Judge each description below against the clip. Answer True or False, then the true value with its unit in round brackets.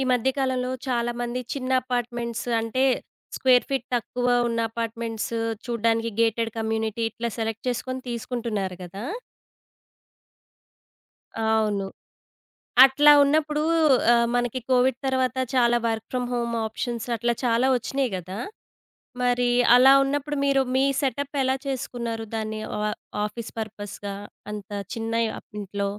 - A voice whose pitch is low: False (235 Hz)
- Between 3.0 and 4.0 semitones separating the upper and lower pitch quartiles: False (2.4 semitones)